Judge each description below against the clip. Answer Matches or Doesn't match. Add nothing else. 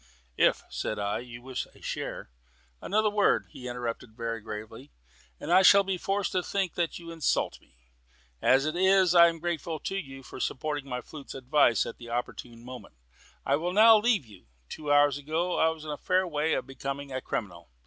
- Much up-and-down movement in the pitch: Matches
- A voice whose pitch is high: Doesn't match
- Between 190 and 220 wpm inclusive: Matches